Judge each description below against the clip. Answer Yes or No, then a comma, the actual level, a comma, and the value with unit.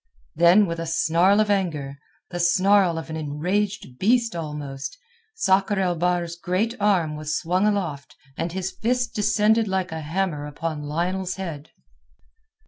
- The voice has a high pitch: No, medium, 175 Hz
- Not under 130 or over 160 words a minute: Yes, average, 145 wpm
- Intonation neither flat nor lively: Yes, average, 3.8 semitones